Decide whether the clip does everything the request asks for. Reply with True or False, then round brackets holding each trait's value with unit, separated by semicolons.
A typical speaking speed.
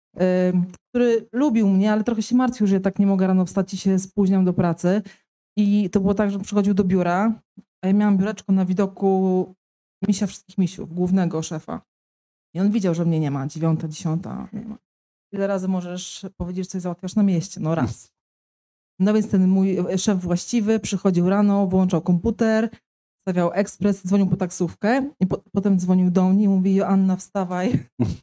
False (185 wpm)